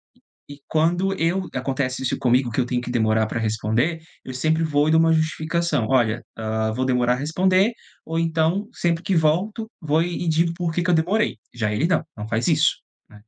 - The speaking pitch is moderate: Yes, medium, 155 Hz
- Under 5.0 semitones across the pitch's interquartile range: No, wide, 5.5 semitones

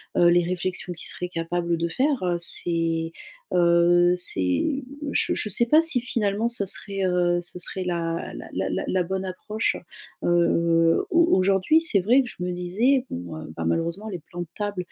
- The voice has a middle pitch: Yes, medium, 180 Hz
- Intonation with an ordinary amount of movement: Yes, average, 3.2 semitones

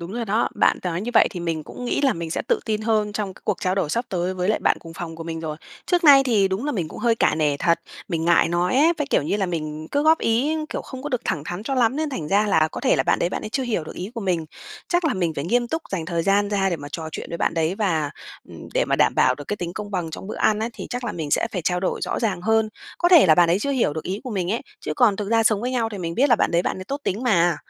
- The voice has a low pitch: No, high, 195 Hz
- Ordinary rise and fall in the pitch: No, wide, 5.7 semitones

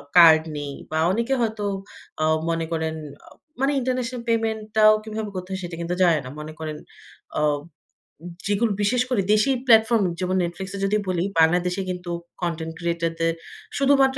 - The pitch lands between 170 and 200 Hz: Yes, high, 190 Hz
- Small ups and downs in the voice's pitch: No, average, 5.1 semitones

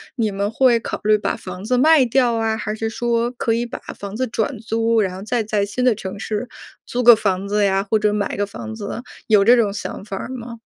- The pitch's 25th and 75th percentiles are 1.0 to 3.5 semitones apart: Yes, average, 2.7 semitones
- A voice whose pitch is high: Yes, high, 220 Hz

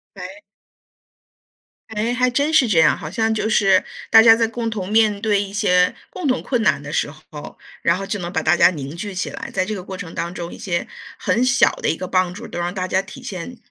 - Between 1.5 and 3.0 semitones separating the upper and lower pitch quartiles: No, average, 4.2 semitones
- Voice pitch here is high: Yes, high, 195 Hz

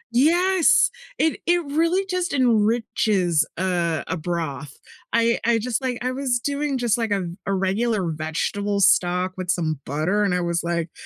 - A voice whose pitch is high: Yes, high, 205 Hz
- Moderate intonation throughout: No, wide, 6.5 semitones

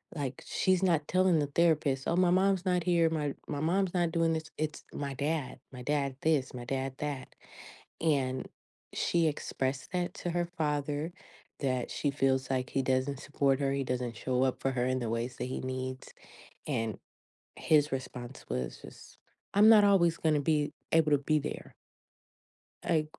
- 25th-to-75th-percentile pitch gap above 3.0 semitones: Yes, average, 3.8 semitones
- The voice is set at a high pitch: No, medium, 145 Hz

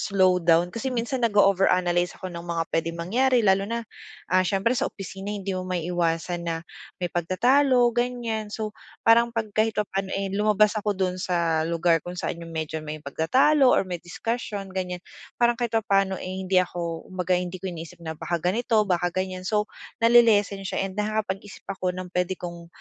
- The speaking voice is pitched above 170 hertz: Yes, high, 190 Hz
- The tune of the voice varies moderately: Yes, average, 3.5 semitones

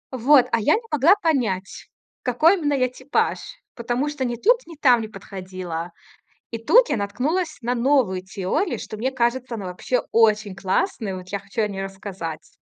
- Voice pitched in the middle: No, high, 235 Hz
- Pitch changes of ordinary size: No, wide, 5.8 semitones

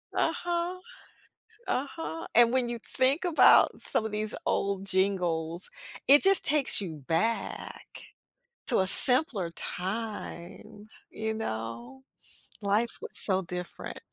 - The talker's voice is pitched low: No, high, 215 Hz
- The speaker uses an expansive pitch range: Yes, wide, 5.9 semitones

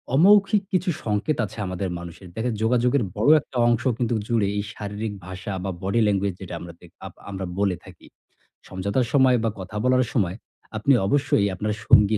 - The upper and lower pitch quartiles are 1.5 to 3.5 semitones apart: No, average, 4.3 semitones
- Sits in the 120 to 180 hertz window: No, low, 105 Hz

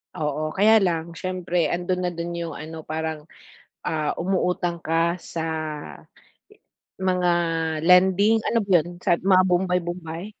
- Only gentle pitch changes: Yes, narrow, 2.2 semitones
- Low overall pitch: No, medium, 175 Hz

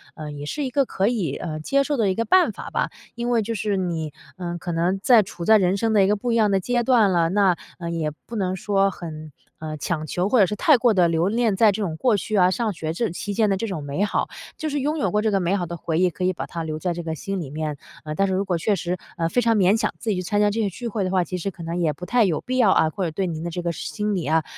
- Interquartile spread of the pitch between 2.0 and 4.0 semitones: No, average, 4.4 semitones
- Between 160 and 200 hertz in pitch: Yes, high, 190 Hz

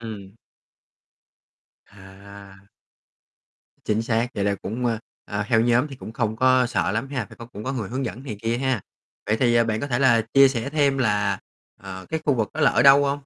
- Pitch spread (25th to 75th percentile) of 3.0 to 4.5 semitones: Yes, average, 4.2 semitones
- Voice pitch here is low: Yes, low, 115 Hz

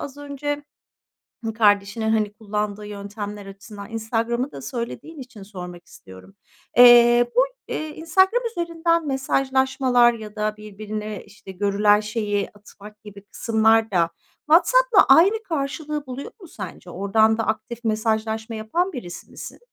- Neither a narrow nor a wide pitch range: Yes, average, 4.6 semitones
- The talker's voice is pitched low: No, high, 220 Hz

